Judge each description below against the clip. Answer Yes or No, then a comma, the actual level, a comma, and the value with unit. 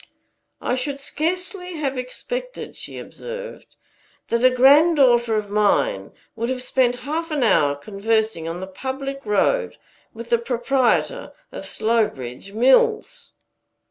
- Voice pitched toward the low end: No, very high, 255 Hz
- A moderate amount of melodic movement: No, wide, 6.1 semitones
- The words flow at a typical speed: No, slow, 125 wpm